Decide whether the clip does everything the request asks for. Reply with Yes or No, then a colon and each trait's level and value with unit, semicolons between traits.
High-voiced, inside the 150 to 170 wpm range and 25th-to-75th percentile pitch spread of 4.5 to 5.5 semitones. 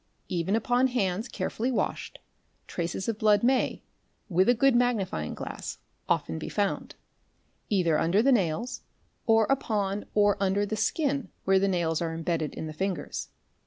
Yes: high, 200 Hz; average, 160 wpm; average, 5.1 semitones